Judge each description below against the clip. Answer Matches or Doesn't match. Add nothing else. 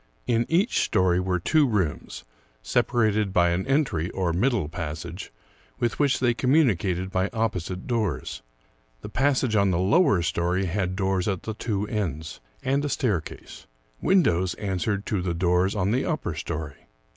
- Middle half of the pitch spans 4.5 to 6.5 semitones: Matches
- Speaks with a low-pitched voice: Matches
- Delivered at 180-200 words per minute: Doesn't match